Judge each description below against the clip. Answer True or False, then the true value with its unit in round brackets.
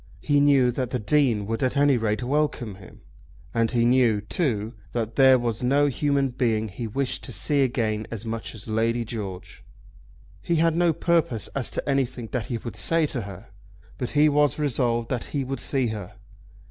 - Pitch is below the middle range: True (125 Hz)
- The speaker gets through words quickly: False (190 wpm)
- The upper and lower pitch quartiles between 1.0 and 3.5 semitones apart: False (3.9 semitones)